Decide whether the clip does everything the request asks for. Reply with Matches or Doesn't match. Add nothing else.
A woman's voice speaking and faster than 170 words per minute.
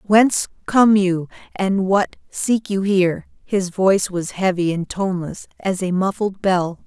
Doesn't match